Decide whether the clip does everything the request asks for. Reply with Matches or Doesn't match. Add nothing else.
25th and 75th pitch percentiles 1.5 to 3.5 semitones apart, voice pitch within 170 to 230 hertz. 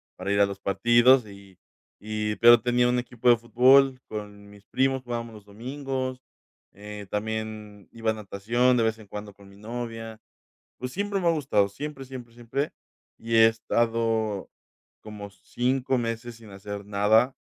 Doesn't match